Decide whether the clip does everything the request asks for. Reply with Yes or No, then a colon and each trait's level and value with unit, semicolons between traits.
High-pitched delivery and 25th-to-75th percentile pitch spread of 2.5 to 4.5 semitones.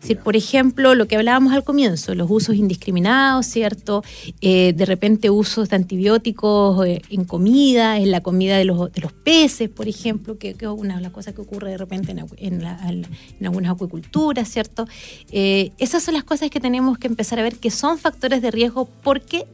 No: high, 215 Hz; average, 4.9 semitones